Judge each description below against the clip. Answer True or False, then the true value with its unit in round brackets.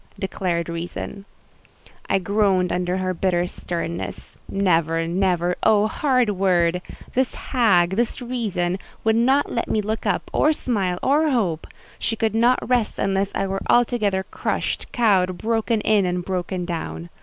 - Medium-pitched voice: False (195 Hz)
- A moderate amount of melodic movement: True (4.1 semitones)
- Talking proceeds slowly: False (145 wpm)